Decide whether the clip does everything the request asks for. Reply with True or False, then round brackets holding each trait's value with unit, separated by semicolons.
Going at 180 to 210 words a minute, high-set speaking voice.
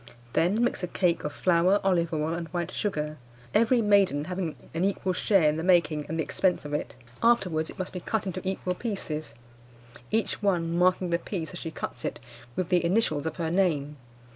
False (200 wpm; 175 Hz)